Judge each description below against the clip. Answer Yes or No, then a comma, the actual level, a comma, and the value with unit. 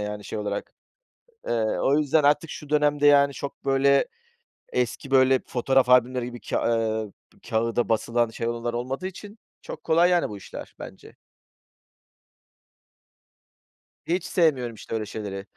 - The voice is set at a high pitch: No, low, 130 Hz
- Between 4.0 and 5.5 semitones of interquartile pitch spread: Yes, average, 4.3 semitones